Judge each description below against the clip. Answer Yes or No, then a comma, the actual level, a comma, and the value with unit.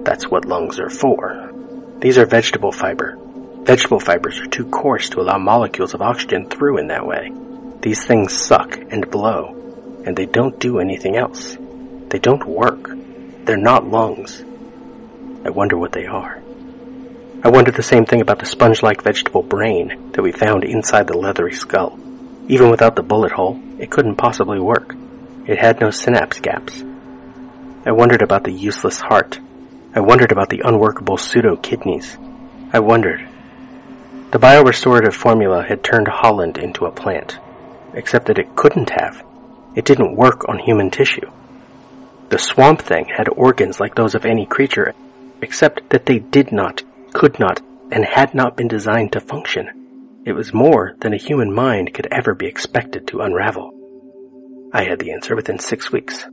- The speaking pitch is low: No, high, 240 Hz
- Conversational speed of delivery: Yes, average, 165 wpm